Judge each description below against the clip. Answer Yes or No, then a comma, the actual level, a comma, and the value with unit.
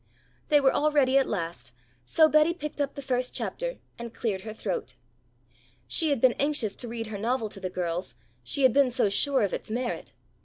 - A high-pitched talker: Yes, high, 245 Hz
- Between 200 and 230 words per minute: Yes, fast, 205 wpm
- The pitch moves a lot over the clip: Yes, wide, 5.7 semitones